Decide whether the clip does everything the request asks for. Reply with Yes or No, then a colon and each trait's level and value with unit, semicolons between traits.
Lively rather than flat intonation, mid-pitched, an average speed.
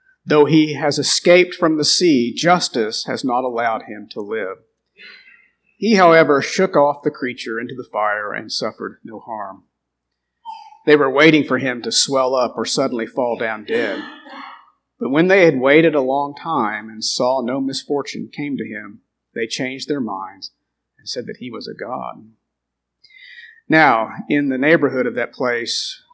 Yes: wide, 8.3 semitones; medium, 150 Hz; average, 170 wpm